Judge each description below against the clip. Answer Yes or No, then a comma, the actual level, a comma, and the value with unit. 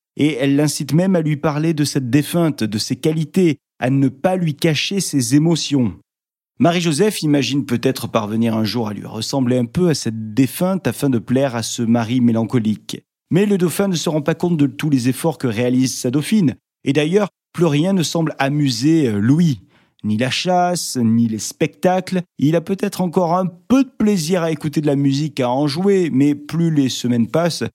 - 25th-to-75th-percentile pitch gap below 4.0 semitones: No, average, 5.2 semitones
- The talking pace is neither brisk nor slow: Yes, average, 200 wpm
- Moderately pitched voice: Yes, medium, 150 Hz